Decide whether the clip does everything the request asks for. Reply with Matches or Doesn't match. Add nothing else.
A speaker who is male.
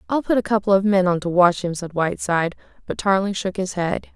Doesn't match